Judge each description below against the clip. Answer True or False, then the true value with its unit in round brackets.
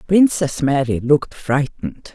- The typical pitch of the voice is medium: True (145 Hz)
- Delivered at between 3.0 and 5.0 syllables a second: True (4.5 syllables/s)